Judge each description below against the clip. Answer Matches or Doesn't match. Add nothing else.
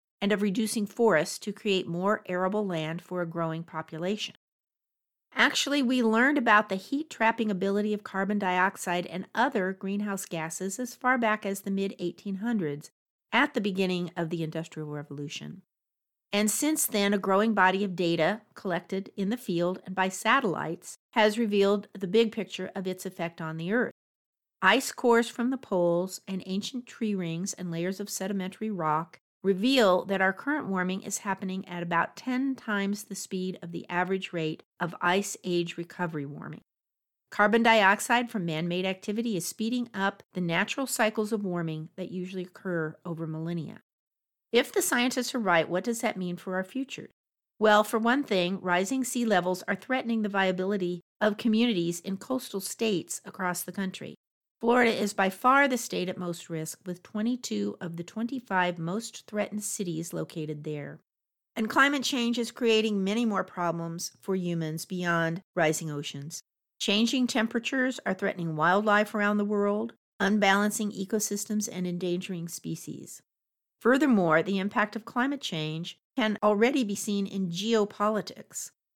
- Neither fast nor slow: Matches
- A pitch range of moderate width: Matches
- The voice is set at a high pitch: Matches